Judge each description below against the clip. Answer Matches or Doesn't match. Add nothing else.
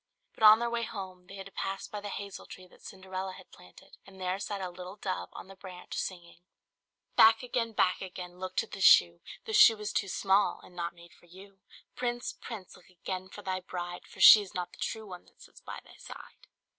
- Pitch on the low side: Doesn't match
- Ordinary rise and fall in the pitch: Doesn't match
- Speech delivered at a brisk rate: Matches